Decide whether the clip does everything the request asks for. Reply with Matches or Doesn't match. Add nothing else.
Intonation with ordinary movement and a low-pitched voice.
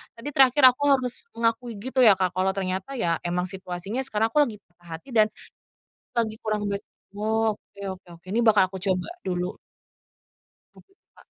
Doesn't match